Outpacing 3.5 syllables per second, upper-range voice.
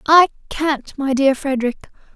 Yes: 4.5 syllables/s; very high, 280 Hz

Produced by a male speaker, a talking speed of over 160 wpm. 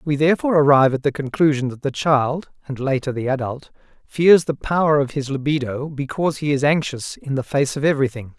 Yes: male; average, 200 wpm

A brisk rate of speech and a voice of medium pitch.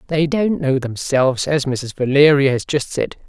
No: average, 165 wpm; medium, 145 Hz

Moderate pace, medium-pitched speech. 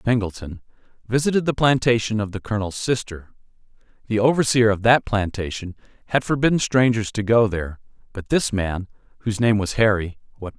No: average, 170 wpm; low, 110 Hz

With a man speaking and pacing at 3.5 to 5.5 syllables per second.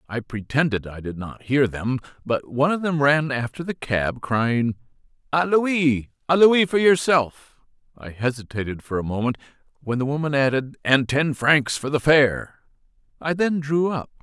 Yes: male; 4.5 syllables/s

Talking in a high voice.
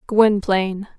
Yes: high, 200 Hz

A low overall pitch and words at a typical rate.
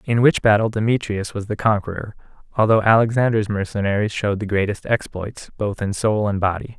Yes: low, 105 Hz; average, 170 wpm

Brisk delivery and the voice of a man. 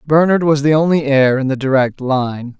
Yes: fast, 210 wpm; male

